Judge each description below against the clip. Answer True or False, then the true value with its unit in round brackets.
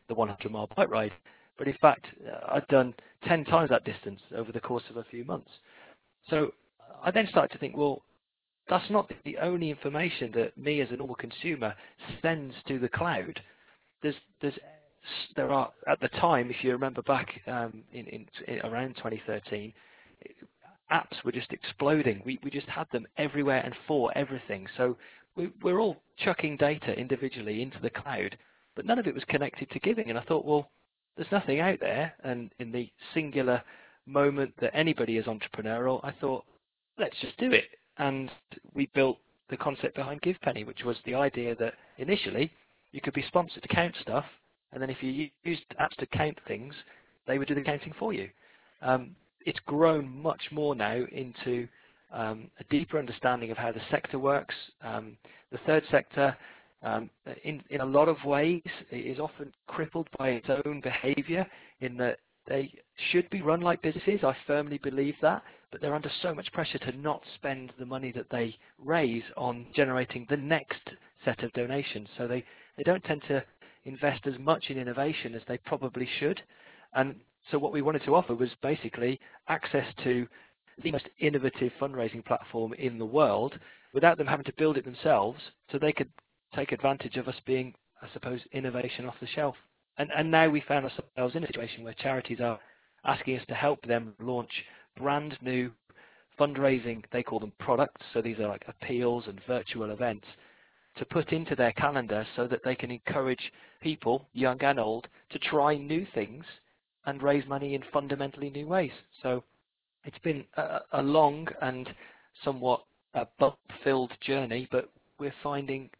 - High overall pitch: False (135 Hz)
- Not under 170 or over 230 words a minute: True (180 wpm)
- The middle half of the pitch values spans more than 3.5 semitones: False (3.1 semitones)